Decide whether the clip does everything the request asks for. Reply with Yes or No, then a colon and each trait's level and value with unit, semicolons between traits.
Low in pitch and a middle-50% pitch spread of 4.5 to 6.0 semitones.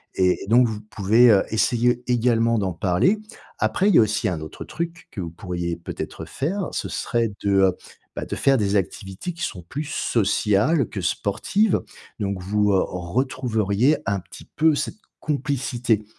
Yes: low, 110 Hz; wide, 5.5 semitones